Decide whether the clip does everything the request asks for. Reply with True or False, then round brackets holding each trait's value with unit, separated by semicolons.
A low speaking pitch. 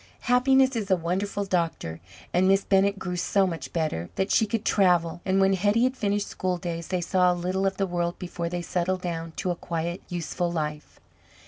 False (180 Hz)